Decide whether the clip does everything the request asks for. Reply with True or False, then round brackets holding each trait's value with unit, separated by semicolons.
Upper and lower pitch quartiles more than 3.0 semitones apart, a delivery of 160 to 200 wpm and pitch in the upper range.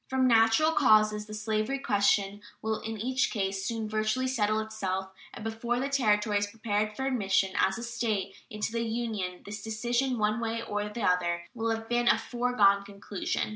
False (2.6 semitones; 180 wpm; 220 Hz)